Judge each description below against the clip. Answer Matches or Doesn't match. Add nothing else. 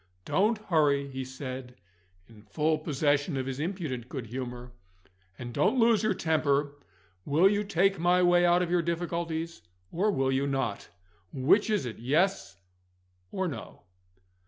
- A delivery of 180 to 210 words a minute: Doesn't match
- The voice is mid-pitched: Matches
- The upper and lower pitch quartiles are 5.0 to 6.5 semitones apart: Matches